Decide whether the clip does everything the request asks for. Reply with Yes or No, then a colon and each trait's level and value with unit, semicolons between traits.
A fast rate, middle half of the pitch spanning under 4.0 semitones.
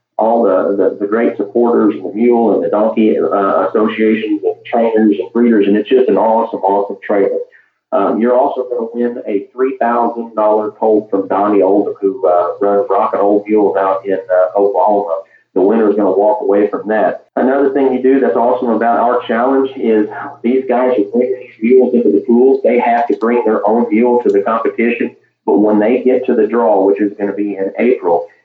Yes: fast, 210 wpm; average, 3.6 semitones